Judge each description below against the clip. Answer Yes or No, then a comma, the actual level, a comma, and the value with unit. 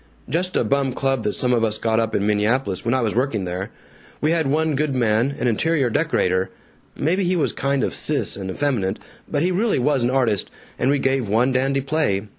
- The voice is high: No, low, 130 Hz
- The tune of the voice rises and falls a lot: No, average, 4.7 semitones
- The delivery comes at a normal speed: No, fast, 220 wpm